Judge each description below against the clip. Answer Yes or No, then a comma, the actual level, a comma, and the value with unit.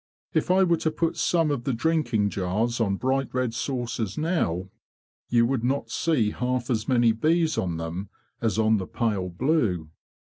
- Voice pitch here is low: Yes, low, 120 Hz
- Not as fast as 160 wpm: No, average, 175 wpm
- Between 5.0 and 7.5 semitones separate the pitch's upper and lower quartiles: Yes, wide, 5.6 semitones